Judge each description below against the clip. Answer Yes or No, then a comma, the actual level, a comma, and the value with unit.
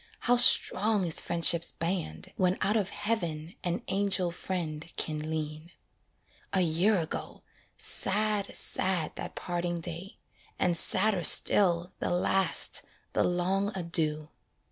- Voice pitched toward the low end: No, medium, 175 Hz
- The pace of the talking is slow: Yes, slow, 120 wpm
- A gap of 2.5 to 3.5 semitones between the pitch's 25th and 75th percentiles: Yes, average, 2.9 semitones